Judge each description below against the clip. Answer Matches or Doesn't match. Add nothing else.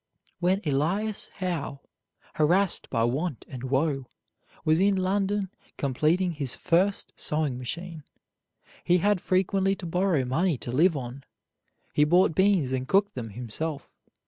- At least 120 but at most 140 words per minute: Matches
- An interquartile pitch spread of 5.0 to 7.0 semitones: Matches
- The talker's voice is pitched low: Doesn't match